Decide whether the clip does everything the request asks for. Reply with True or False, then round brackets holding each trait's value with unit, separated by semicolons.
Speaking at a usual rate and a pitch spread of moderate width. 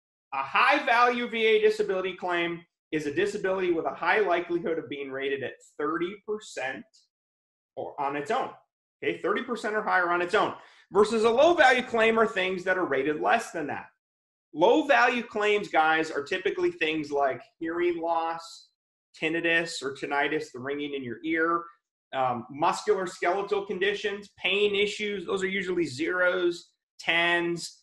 True (155 wpm; 4.2 semitones)